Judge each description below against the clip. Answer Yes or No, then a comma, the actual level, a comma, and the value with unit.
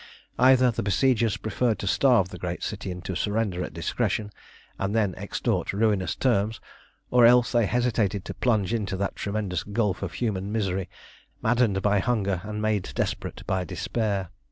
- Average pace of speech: Yes, average, 160 wpm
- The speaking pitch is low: Yes, low, 105 Hz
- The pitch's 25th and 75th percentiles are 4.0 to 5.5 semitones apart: No, average, 3.2 semitones